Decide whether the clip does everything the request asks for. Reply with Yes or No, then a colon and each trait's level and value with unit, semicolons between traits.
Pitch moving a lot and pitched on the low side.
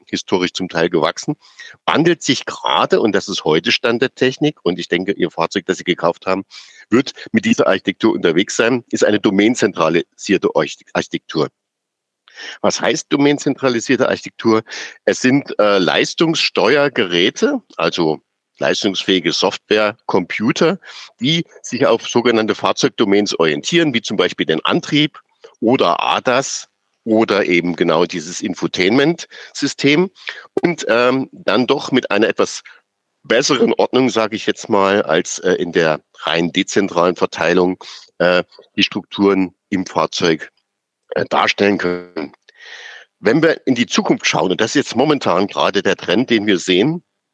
Yes: wide, 7.1 semitones; low, 110 Hz